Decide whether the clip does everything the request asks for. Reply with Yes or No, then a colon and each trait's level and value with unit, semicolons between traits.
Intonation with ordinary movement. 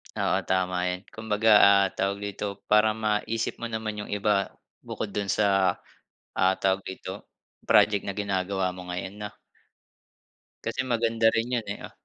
No: narrow, 2.2 semitones